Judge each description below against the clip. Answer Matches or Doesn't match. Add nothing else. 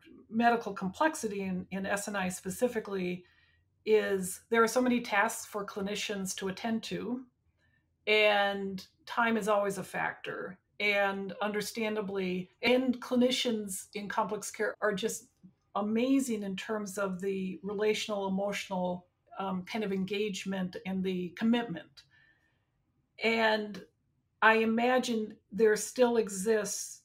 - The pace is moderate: Doesn't match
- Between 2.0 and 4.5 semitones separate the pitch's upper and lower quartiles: Matches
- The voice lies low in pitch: Doesn't match